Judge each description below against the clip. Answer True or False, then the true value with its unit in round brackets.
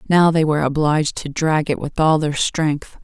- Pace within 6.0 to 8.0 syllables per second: False (4.9 syllables/s)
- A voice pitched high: False (155 Hz)